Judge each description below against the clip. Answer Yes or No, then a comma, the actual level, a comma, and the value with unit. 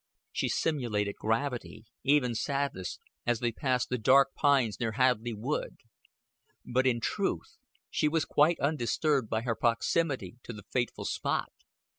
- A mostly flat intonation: No, average, 3.7 semitones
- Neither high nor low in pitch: No, low, 125 Hz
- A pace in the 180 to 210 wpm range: No, average, 140 wpm